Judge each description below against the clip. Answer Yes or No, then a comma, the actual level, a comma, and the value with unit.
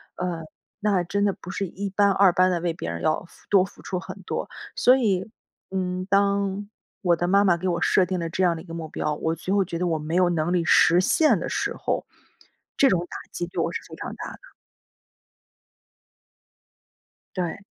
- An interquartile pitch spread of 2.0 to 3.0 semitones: Yes, narrow, 2.5 semitones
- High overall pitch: No, medium, 180 Hz